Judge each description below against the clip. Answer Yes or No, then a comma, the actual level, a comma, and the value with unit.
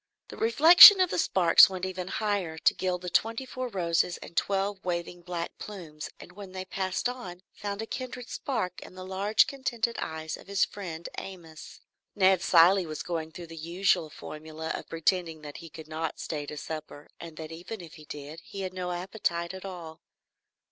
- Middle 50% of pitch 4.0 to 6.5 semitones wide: No, average, 3.4 semitones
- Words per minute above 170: Yes, average, 190 wpm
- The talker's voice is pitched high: No, medium, 180 Hz